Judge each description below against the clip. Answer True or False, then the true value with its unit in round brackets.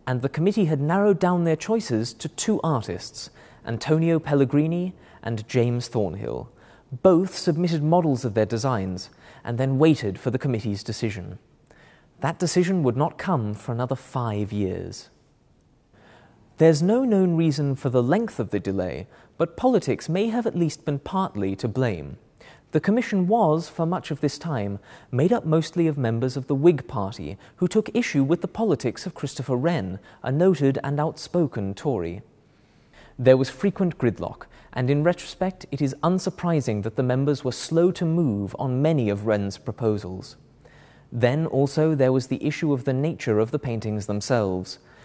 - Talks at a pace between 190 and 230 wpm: False (165 wpm)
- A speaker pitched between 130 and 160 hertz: True (140 Hz)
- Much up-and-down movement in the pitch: True (6.5 semitones)